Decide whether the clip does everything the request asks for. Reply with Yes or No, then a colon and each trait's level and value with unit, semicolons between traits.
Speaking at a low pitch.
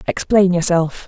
No: medium, 180 Hz